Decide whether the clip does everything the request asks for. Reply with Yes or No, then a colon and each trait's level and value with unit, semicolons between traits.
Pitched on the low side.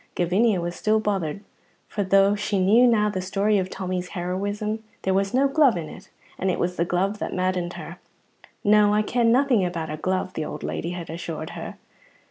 No: high, 195 Hz